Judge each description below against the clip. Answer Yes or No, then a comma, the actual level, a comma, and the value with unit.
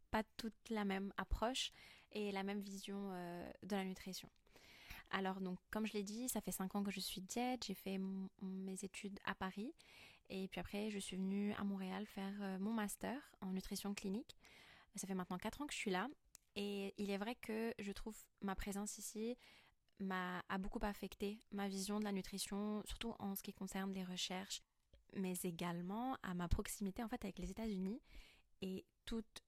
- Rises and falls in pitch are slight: Yes, narrow, 1.8 semitones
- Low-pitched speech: No, high, 200 Hz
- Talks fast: No, average, 195 wpm